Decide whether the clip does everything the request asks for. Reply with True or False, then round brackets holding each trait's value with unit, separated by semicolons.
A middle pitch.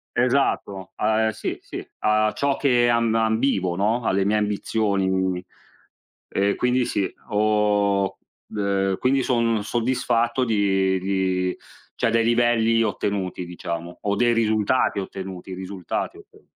False (105 Hz)